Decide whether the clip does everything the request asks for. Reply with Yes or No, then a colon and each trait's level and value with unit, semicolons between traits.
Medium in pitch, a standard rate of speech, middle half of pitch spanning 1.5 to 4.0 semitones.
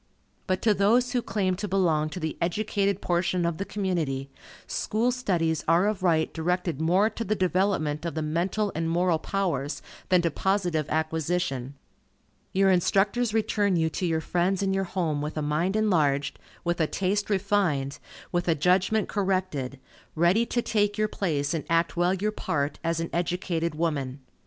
Yes: medium, 175 Hz; average, 170 wpm; average, 3.7 semitones